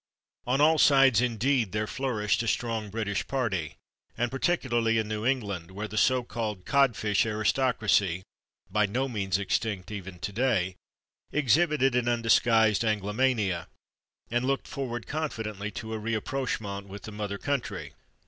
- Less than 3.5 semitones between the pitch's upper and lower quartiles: No, average, 3.9 semitones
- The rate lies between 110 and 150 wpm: Yes, average, 140 wpm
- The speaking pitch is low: Yes, low, 110 Hz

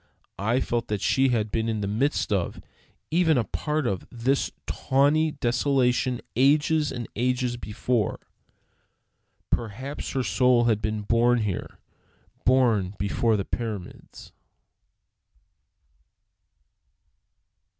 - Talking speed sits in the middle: No, slow, 110 wpm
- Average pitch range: Yes, average, 3.6 semitones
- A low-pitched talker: Yes, low, 120 Hz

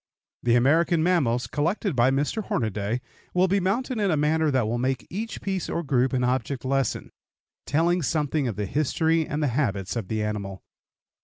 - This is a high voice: No, medium, 140 Hz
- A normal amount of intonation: No, wide, 5.8 semitones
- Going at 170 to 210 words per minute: Yes, average, 180 wpm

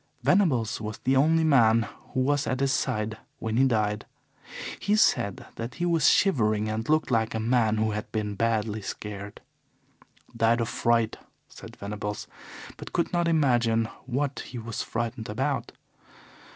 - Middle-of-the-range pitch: No, low, 115 Hz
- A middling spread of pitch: Yes, average, 3.8 semitones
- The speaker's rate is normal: Yes, average, 155 wpm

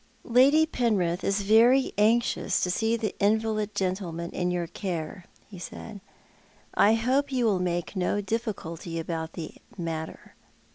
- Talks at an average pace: Yes, average, 150 wpm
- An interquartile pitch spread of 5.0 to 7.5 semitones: No, average, 4.5 semitones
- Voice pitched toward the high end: Yes, high, 200 Hz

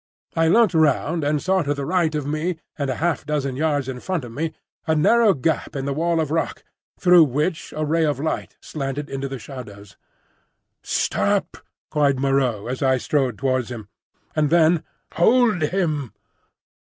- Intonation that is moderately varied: Yes, average, 3.3 semitones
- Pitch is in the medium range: Yes, medium, 150 Hz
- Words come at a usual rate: Yes, average, 175 wpm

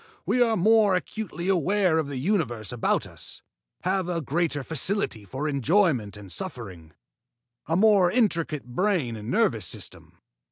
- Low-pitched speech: No, medium, 165 Hz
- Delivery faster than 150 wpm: No, average, 145 wpm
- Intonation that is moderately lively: No, wide, 8.0 semitones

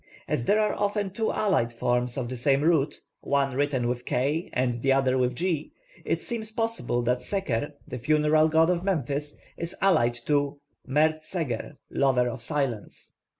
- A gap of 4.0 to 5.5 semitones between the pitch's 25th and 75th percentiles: Yes, average, 5.1 semitones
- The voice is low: No, medium, 145 Hz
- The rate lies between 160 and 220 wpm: Yes, average, 170 wpm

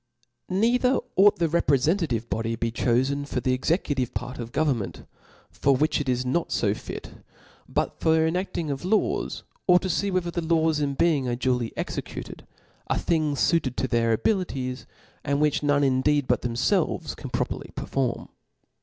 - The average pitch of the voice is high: No, medium, 145 Hz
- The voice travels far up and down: No, average, 4.8 semitones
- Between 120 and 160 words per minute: No, average, 170 wpm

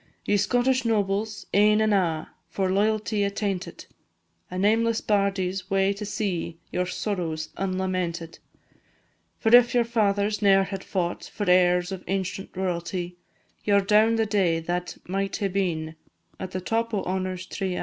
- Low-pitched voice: No, high, 195 Hz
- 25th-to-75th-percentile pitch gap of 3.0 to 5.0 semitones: No, narrow, 2.4 semitones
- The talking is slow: No, average, 160 wpm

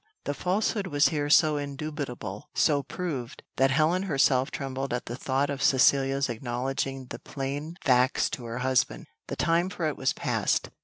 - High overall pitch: No, low, 135 Hz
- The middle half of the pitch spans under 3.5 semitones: Yes, average, 2.7 semitones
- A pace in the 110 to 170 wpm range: Yes, average, 165 wpm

